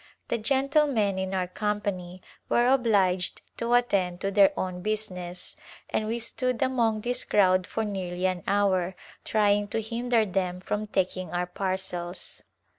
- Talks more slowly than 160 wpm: Yes, average, 145 wpm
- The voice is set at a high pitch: Yes, high, 200 Hz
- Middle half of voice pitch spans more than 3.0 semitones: Yes, average, 3.4 semitones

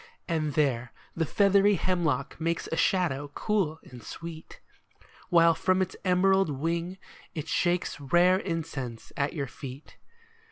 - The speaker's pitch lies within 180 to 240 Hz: No, medium, 165 Hz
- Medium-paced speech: No, slow, 130 wpm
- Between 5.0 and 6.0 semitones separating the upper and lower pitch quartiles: No, average, 4.1 semitones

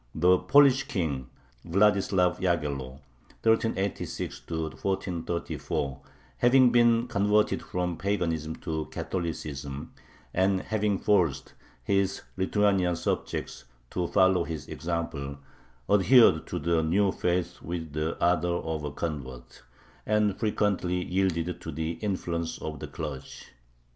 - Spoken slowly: Yes, slow, 110 wpm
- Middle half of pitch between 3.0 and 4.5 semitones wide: Yes, average, 3.9 semitones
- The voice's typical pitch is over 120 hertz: No, very low, 90 Hz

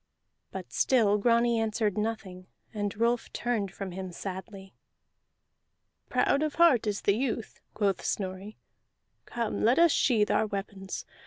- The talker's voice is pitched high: Yes, high, 215 Hz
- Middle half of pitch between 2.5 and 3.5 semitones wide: Yes, average, 3.1 semitones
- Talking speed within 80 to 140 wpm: Yes, slow, 135 wpm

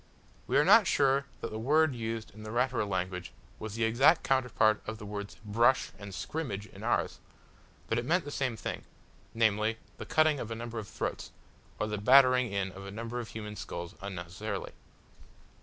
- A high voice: No, low, 110 Hz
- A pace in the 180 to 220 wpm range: Yes, average, 190 wpm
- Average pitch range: Yes, average, 3.7 semitones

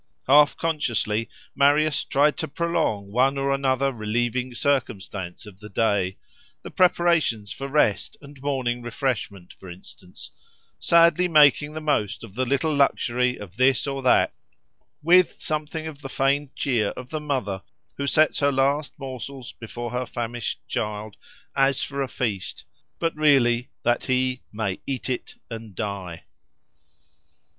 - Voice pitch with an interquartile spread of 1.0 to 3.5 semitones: No, average, 4.3 semitones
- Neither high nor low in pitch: No, low, 130 Hz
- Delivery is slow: No, average, 145 wpm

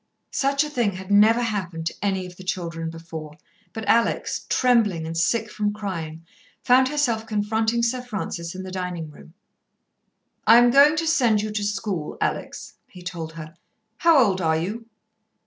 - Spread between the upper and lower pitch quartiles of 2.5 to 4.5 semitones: No, wide, 5.6 semitones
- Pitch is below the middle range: No, high, 205 Hz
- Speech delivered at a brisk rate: No, average, 170 wpm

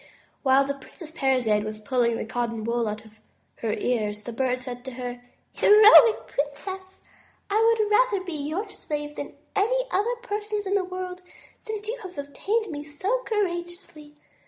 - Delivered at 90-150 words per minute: No, average, 165 wpm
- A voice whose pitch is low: No, very high, 305 Hz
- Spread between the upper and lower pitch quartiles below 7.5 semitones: No, wide, 8.7 semitones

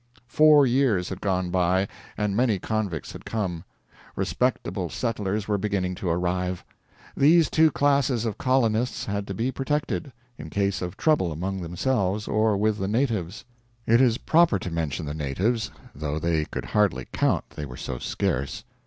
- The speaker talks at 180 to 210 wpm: No, average, 160 wpm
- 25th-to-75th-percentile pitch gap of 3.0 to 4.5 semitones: No, average, 5.0 semitones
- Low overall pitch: Yes, low, 100 Hz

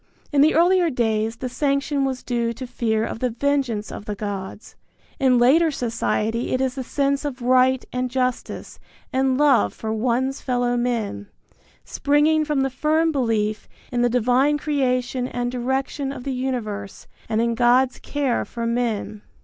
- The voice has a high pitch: Yes, very high, 250 Hz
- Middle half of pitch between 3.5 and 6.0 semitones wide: No, average, 2.8 semitones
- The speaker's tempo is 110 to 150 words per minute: No, average, 165 wpm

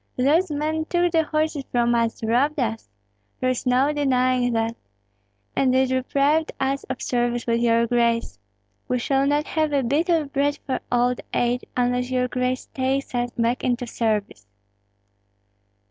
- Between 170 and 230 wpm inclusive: No, average, 160 wpm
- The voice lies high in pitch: Yes, very high, 255 Hz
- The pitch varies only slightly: No, average, 3.0 semitones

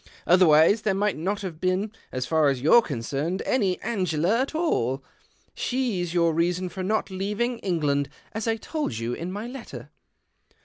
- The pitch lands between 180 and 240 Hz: Yes, medium, 185 Hz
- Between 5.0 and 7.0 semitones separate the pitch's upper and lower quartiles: Yes, wide, 5.4 semitones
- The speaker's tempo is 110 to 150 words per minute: No, average, 165 wpm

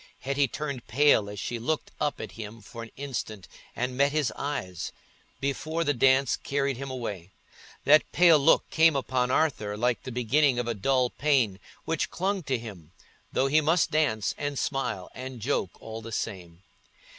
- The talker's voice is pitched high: No, low, 130 Hz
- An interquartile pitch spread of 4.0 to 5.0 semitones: Yes, average, 4.4 semitones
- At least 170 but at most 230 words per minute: Yes, average, 175 wpm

